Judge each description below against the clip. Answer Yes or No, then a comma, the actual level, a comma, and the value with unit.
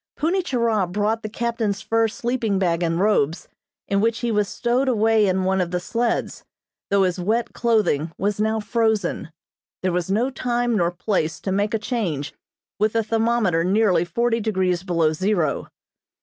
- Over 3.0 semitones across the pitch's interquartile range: Yes, average, 4.0 semitones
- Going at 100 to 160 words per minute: No, average, 170 wpm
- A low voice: No, high, 210 Hz